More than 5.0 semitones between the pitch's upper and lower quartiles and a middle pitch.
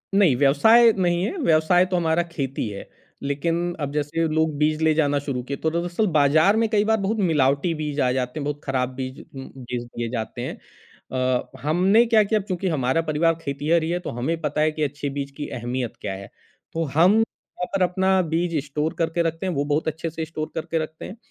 No: average, 3.9 semitones; medium, 155 Hz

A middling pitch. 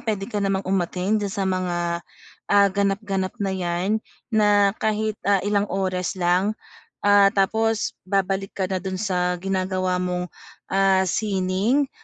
No: high, 195 Hz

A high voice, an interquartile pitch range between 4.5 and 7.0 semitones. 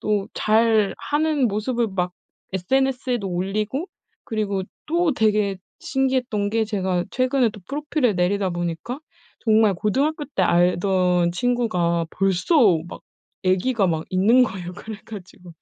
Yes: high, 210 Hz; average, 5.3 semitones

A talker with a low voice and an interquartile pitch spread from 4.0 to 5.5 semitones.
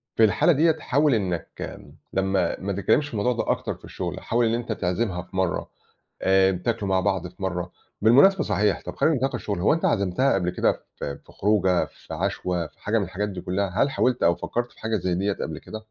Yes: low, 100 Hz; average, 4.4 semitones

